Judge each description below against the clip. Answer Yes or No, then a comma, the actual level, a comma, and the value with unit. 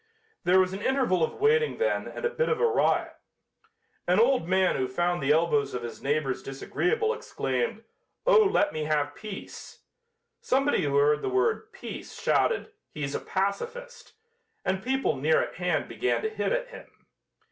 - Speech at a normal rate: Yes, average, 170 wpm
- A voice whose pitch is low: No, high, 190 Hz